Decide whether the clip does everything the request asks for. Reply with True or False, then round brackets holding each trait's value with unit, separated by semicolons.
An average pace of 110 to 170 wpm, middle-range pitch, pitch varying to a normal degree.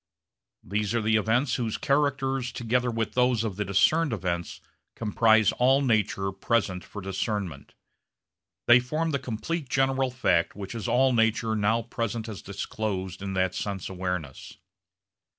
False (145 wpm; 110 Hz; 4.3 semitones)